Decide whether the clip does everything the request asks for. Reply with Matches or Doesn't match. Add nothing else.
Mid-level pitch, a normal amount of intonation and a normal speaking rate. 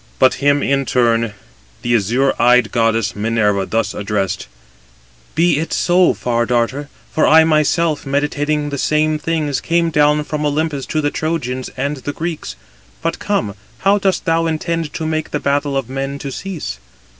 Matches